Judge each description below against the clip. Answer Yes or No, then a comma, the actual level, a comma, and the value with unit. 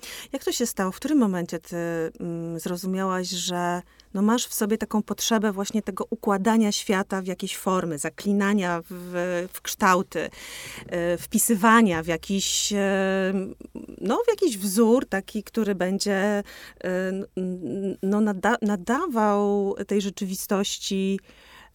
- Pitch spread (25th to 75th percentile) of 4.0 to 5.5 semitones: No, average, 3.0 semitones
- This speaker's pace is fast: No, average, 115 wpm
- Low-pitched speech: No, high, 200 Hz